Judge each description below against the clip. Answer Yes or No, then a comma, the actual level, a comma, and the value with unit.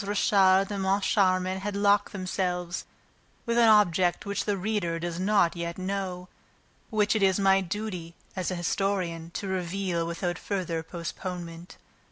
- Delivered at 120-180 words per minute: Yes, average, 150 wpm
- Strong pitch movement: No, narrow, 2.5 semitones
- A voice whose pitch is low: No, medium, 185 Hz